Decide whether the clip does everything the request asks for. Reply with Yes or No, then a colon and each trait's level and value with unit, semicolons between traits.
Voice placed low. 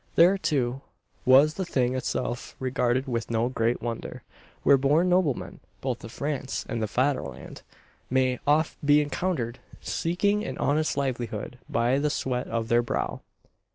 Yes: low, 130 Hz